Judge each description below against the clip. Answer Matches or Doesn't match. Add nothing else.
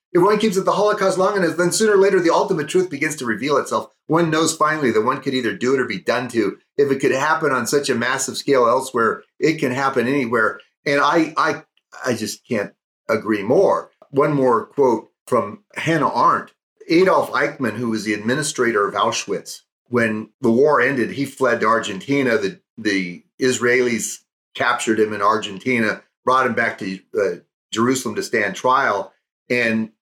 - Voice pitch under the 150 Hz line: Matches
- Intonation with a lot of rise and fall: Matches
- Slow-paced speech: Doesn't match